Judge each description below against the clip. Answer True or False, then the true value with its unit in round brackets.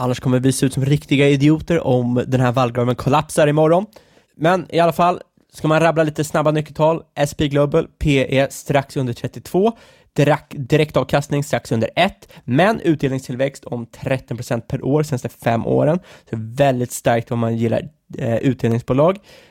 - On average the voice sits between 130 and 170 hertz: True (140 Hz)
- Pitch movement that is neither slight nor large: True (3.5 semitones)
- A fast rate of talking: False (165 wpm)